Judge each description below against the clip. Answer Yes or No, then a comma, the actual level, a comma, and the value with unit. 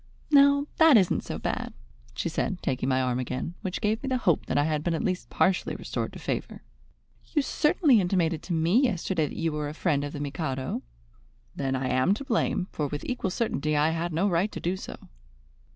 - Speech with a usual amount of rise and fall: No, wide, 6.0 semitones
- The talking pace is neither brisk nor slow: No, fast, 215 wpm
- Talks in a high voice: No, medium, 170 Hz